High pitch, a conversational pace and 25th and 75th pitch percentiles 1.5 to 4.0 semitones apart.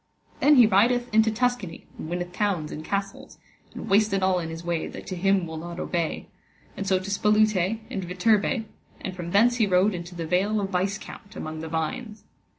Yes: high, 195 Hz; average, 195 wpm; average, 3.7 semitones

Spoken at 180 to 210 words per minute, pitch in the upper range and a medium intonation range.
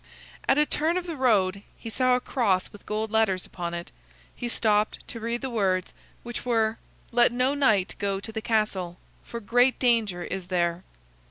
Yes: average, 185 wpm; high, 220 Hz; average, 4.2 semitones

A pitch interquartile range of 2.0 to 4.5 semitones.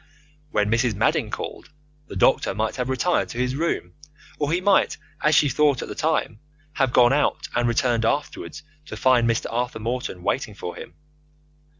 Yes: average, 4.1 semitones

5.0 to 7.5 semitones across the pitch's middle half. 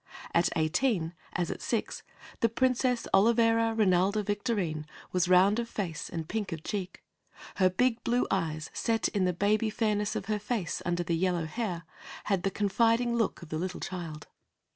No: average, 4.5 semitones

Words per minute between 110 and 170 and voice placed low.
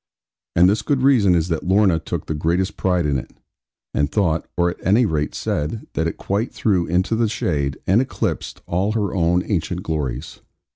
No: average, 190 wpm; very low, 90 Hz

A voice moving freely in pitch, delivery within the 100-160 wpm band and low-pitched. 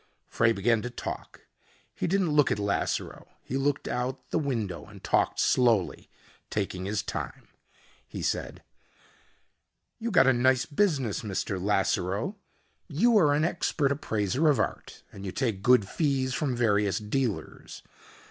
Yes: wide, 5.7 semitones; average, 145 wpm; low, 125 Hz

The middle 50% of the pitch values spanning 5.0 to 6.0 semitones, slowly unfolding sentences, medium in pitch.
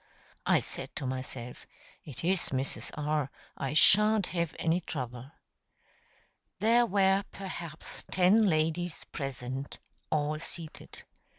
Yes: wide, 5.4 semitones; slow, 110 wpm; medium, 160 Hz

